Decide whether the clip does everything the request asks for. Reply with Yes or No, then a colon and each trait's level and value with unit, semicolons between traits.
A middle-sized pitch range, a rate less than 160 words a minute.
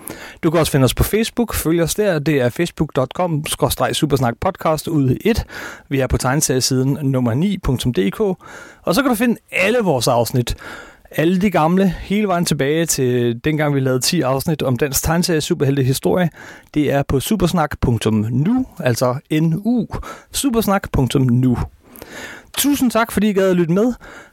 No: wide, 6.3 semitones; average, 150 wpm